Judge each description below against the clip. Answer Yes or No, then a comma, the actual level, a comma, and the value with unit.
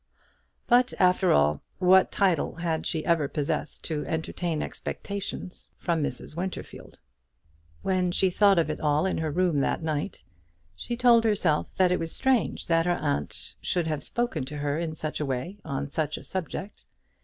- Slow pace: No, average, 170 wpm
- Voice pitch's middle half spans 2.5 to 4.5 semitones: Yes, average, 3.8 semitones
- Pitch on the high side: No, medium, 165 Hz